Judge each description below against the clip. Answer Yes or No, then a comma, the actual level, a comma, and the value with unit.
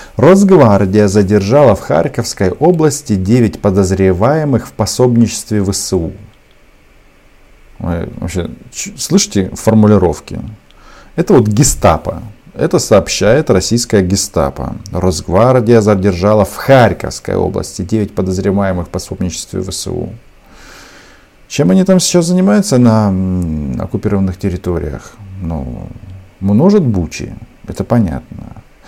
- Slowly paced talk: Yes, slow, 85 wpm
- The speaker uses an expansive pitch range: No, average, 4.0 semitones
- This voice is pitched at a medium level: No, low, 105 Hz